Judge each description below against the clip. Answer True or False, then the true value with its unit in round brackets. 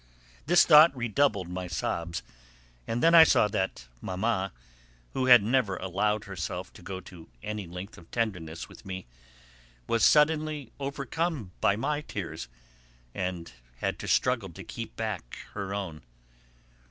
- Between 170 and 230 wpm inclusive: False (140 wpm)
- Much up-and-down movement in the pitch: True (6.0 semitones)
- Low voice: True (105 Hz)